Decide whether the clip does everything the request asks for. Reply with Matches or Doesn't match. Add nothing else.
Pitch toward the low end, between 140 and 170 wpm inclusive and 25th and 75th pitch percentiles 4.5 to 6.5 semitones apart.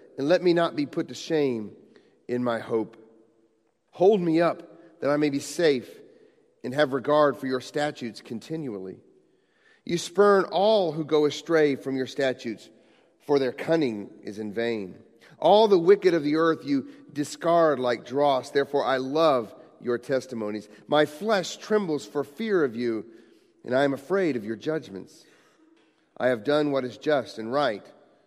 Doesn't match